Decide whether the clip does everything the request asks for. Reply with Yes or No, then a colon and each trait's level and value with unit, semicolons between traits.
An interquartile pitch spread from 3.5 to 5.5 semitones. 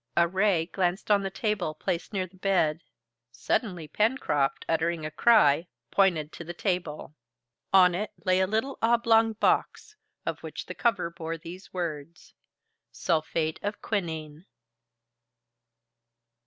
Yes: average, 4.0 semitones